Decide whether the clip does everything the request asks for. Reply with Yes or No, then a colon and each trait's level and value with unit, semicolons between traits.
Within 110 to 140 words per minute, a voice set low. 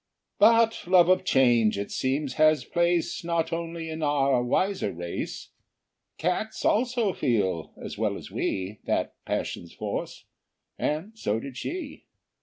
No: slow, 135 wpm; medium, 155 Hz